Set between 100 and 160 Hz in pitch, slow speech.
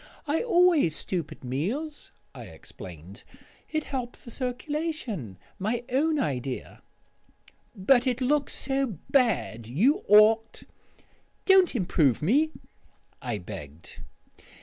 No: high, 235 Hz; slow, 110 wpm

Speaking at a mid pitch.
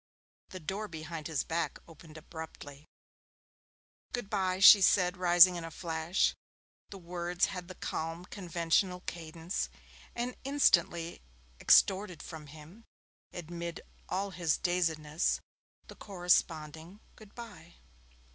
Yes: medium, 175 Hz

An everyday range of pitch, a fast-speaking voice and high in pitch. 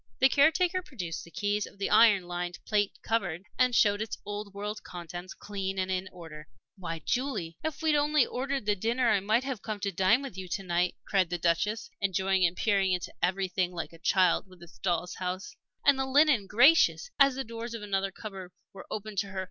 Yes: average, 4.3 semitones; fast, 210 wpm; high, 200 Hz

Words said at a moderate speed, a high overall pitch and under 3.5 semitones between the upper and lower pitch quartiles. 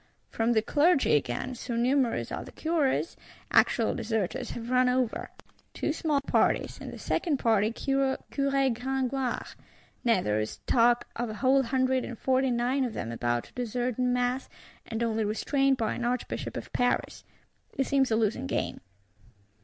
Yes: average, 165 wpm; very high, 250 Hz; average, 2.9 semitones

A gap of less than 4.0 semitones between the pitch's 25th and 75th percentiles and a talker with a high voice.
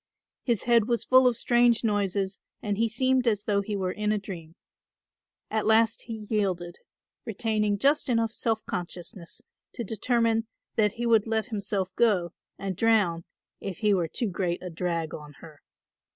Yes: average, 3.5 semitones; high, 210 Hz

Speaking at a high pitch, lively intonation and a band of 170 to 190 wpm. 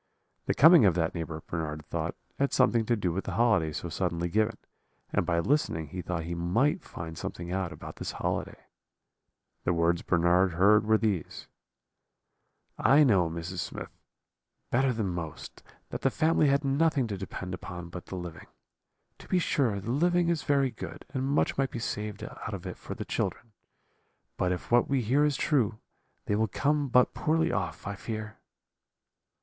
No: low, 105 Hz; wide, 7.6 semitones; average, 180 wpm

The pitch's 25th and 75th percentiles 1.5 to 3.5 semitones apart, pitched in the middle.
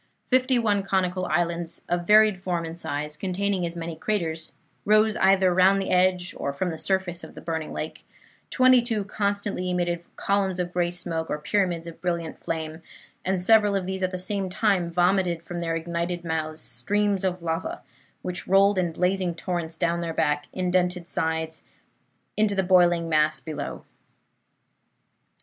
Yes: narrow, 2.6 semitones; medium, 180 Hz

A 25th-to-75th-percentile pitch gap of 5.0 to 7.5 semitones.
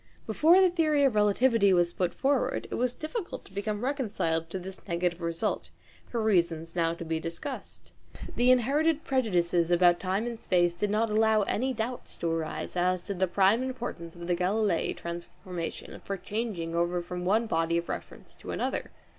Yes: wide, 5.5 semitones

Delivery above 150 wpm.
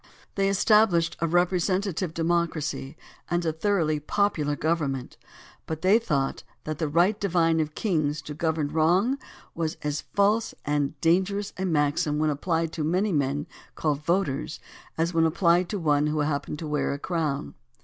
Yes: average, 165 wpm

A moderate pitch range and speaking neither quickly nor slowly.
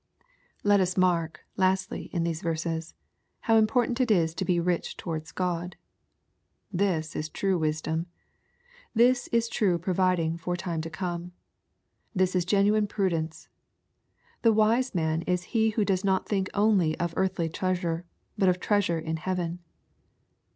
Yes: average, 3.2 semitones; average, 145 wpm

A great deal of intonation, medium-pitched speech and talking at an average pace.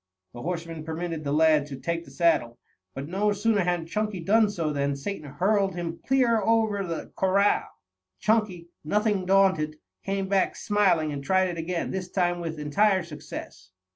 No: average, 4.0 semitones; medium, 175 Hz; average, 170 wpm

